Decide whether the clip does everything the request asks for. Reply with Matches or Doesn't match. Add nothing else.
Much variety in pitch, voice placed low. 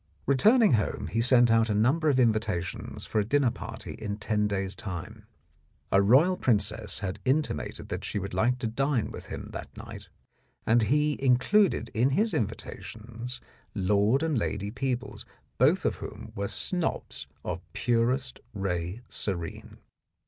Doesn't match